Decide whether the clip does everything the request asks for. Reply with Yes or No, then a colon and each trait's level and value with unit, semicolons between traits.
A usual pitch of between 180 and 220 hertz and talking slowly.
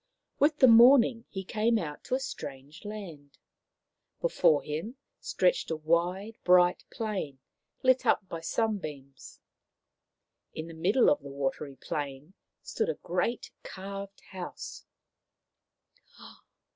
Yes: medium, 185 Hz; slow, 120 wpm